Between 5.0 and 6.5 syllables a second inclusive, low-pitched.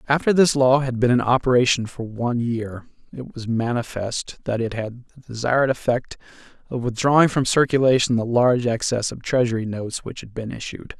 Yes: 5.6 syllables/s; low, 120 Hz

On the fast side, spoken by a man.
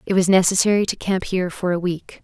No: fast, 240 wpm; female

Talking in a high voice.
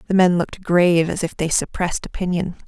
No: medium, 175 Hz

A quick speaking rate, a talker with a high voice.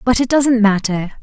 No: average, 195 wpm; high, 225 Hz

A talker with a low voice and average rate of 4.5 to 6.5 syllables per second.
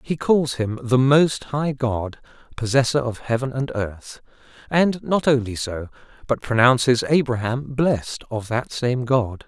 No: low, 125 Hz; 4.1 syllables/s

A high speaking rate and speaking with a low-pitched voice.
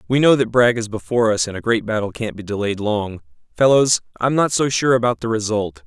Yes: fast, 235 wpm; low, 110 Hz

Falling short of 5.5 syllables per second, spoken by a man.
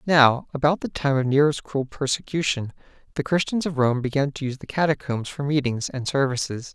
No: 5.6 syllables/s; male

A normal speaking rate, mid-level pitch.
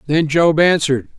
Yes: average, 150 wpm; medium, 155 Hz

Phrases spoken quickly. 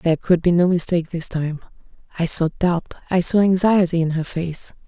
No: average, 195 wpm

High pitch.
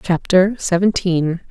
No: medium, 180 Hz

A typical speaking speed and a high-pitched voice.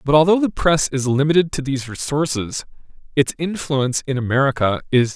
No: average, 175 wpm; medium, 140 Hz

